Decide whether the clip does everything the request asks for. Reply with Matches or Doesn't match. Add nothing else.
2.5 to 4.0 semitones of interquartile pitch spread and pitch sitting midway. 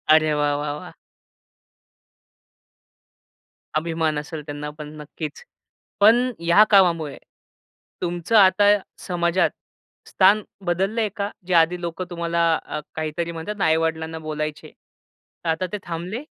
Matches